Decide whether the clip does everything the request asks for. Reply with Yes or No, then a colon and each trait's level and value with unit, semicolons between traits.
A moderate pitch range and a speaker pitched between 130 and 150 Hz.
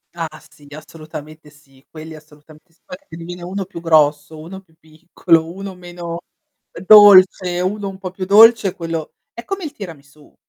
No: average, 3.6 semitones; medium, 170 Hz